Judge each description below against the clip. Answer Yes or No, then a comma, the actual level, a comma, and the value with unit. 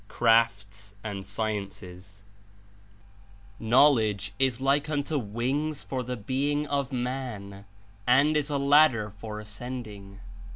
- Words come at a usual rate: No, slow, 115 wpm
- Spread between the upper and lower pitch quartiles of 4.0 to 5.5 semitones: Yes, average, 5.2 semitones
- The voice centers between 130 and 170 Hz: No, low, 115 Hz